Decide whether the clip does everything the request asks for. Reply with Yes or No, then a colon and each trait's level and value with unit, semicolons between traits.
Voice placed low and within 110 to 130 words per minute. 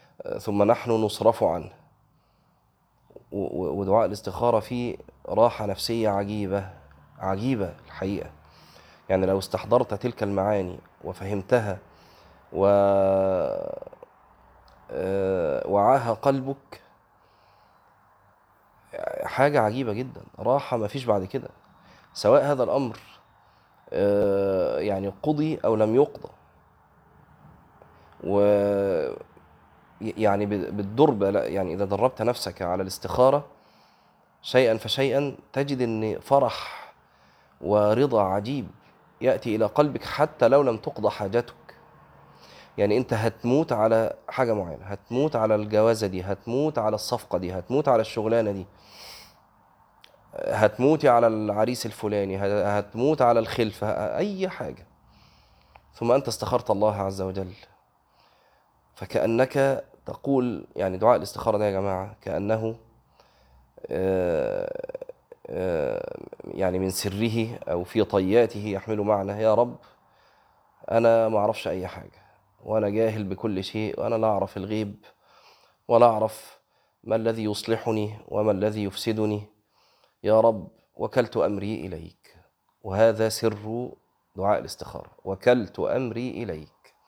No: low, 110 Hz; average, 100 wpm